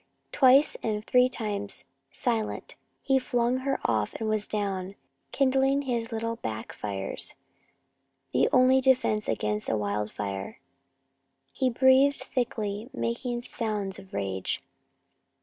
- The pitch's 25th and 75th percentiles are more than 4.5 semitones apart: Yes, wide, 5.5 semitones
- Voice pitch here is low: No, high, 225 Hz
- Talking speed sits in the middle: No, slow, 115 wpm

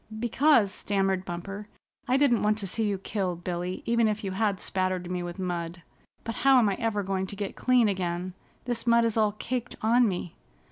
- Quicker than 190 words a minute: Yes, average, 200 wpm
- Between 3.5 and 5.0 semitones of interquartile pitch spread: Yes, average, 3.8 semitones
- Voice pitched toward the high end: Yes, high, 200 Hz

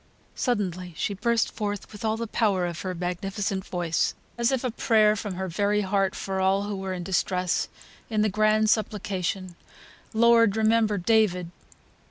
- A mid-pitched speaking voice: No, high, 200 Hz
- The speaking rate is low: No, average, 165 wpm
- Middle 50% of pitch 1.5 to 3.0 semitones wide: Yes, average, 2.7 semitones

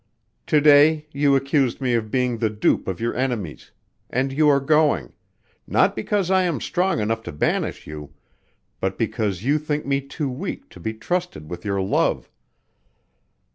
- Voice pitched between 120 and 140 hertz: Yes, low, 135 Hz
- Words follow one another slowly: No, average, 170 wpm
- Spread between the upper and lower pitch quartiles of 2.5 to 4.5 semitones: No, wide, 5.5 semitones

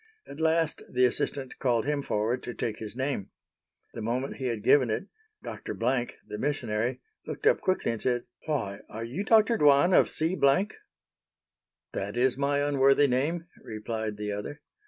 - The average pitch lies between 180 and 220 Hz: No, low, 130 Hz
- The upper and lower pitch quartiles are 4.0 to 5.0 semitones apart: Yes, average, 4.4 semitones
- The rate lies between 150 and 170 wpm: Yes, average, 165 wpm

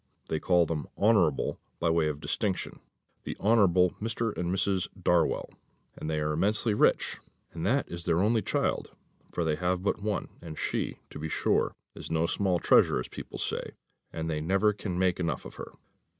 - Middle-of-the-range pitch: No, very low, 90 Hz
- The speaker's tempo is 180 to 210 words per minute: Yes, average, 185 wpm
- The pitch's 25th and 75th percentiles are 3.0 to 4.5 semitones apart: Yes, average, 3.8 semitones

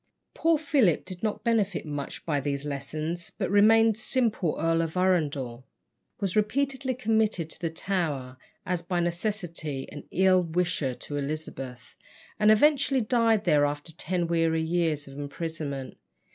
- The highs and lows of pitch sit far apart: Yes, wide, 6.2 semitones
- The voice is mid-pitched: Yes, medium, 170 Hz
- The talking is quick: No, average, 145 wpm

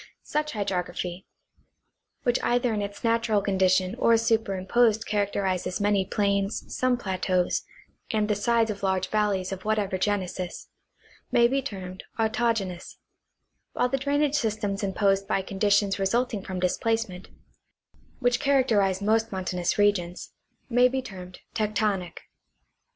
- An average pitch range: Yes, average, 3.2 semitones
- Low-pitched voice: No, high, 205 Hz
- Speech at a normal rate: No, slow, 125 wpm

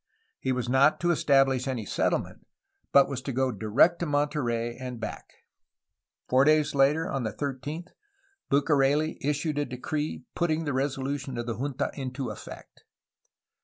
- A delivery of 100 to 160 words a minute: Yes, average, 150 wpm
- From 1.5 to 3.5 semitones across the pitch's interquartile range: Yes, narrow, 2.6 semitones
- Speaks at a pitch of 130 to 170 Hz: Yes, low, 135 Hz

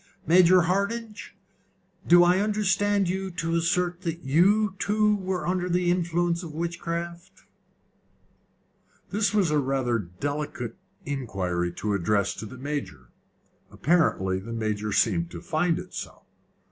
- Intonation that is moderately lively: No, wide, 6.0 semitones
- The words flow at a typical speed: No, slow, 130 wpm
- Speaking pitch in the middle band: Yes, medium, 170 Hz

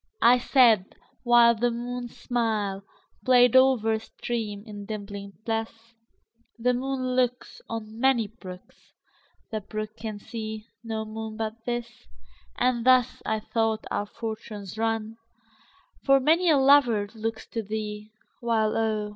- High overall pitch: Yes, high, 225 Hz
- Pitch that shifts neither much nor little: No, narrow, 2.1 semitones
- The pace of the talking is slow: Yes, slow, 110 wpm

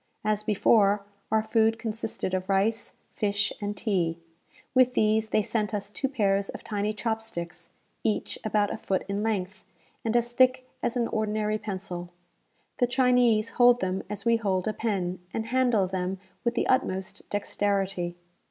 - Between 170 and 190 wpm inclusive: No, average, 160 wpm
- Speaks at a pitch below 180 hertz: No, high, 210 Hz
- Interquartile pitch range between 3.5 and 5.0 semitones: No, narrow, 2.6 semitones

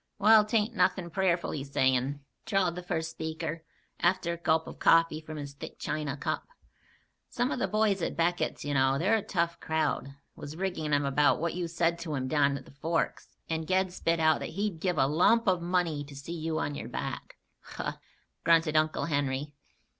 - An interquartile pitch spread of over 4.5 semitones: No, average, 3.4 semitones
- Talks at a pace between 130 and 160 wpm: No, average, 200 wpm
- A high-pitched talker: No, medium, 165 Hz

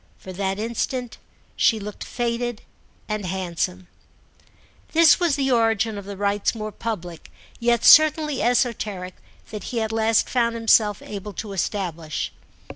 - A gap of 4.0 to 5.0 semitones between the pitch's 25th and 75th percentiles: No, average, 3.4 semitones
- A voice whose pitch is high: Yes, high, 220 Hz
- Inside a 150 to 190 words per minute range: No, slow, 135 wpm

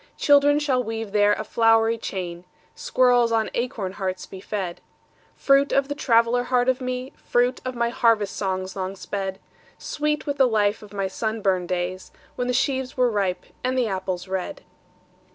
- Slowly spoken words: No, average, 170 wpm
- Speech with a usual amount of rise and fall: Yes, average, 4.7 semitones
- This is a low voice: No, high, 225 Hz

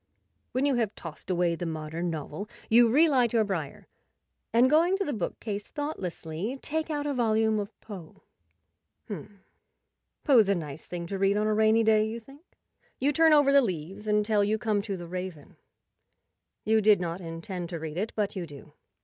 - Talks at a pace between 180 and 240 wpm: Yes, average, 190 wpm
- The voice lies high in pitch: Yes, high, 210 Hz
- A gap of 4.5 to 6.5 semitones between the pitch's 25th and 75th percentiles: Yes, average, 5.2 semitones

